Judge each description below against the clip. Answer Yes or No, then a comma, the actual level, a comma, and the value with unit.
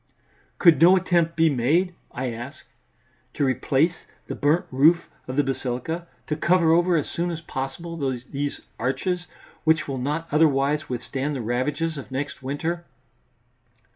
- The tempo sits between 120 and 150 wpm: Yes, average, 145 wpm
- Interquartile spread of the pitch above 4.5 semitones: No, average, 4.0 semitones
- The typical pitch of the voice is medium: Yes, medium, 150 Hz